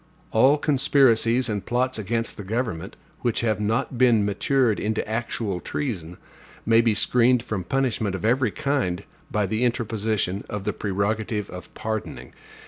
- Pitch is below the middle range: Yes, low, 110 Hz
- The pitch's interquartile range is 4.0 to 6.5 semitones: No, average, 3.2 semitones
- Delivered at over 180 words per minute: No, average, 145 wpm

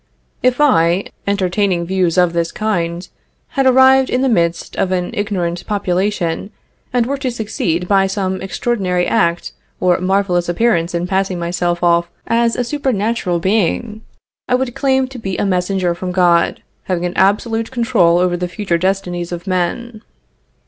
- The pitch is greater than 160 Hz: Yes, high, 190 Hz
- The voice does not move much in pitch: No, average, 4.5 semitones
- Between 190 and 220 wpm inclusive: No, average, 155 wpm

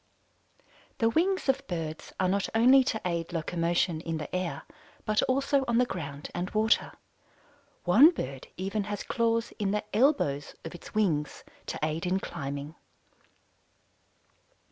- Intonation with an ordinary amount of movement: No, wide, 5.8 semitones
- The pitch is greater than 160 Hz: Yes, high, 190 Hz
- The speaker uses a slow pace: No, average, 145 wpm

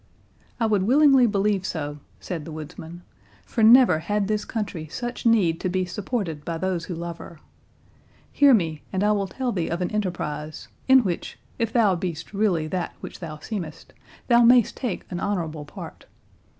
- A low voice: No, medium, 185 Hz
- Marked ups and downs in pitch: No, average, 5.0 semitones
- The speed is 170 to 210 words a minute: Yes, average, 175 wpm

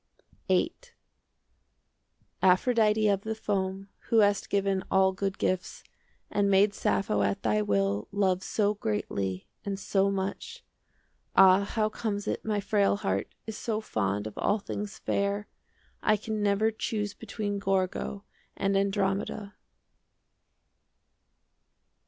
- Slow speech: Yes, slow, 125 wpm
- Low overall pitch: No, high, 200 Hz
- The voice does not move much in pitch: Yes, narrow, 1.8 semitones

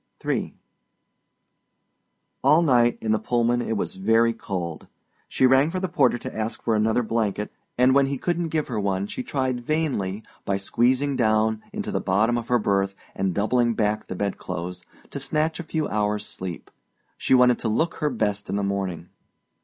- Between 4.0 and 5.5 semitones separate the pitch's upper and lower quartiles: Yes, average, 4.4 semitones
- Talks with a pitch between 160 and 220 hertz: No, low, 115 Hz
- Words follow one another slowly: No, average, 180 wpm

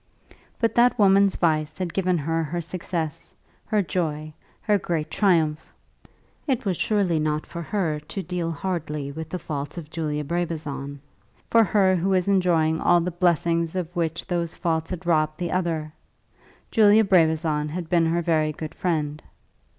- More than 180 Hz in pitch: No, medium, 170 Hz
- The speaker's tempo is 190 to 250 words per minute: No, average, 160 wpm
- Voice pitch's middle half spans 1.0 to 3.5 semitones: Yes, average, 2.9 semitones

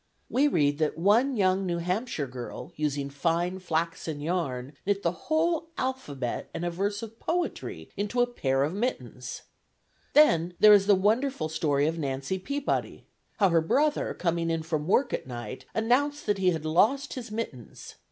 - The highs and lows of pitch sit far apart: Yes, wide, 6.8 semitones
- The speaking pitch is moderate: Yes, medium, 180 Hz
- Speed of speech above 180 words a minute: No, average, 170 wpm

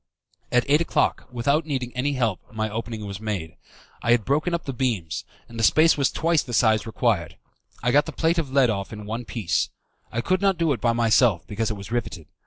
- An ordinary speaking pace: No, fast, 220 wpm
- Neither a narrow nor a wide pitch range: Yes, average, 4.6 semitones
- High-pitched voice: No, low, 120 Hz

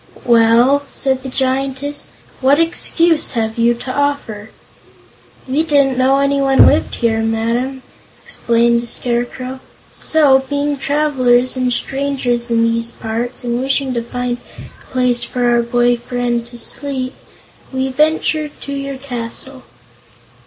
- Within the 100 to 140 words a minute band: Yes, slow, 135 wpm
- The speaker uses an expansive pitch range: No, average, 2.7 semitones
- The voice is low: No, very high, 255 Hz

